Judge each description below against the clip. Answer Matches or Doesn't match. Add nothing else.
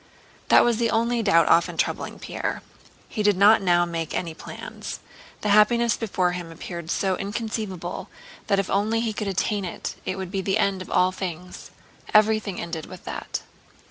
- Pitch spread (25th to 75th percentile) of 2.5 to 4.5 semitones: Matches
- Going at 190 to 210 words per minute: Doesn't match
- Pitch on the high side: Matches